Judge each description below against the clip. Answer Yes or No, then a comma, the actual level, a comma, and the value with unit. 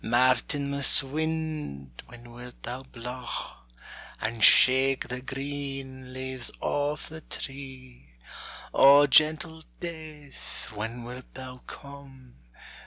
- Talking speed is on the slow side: Yes, slow, 100 wpm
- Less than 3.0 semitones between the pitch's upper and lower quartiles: Yes, narrow, 2.5 semitones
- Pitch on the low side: Yes, low, 130 Hz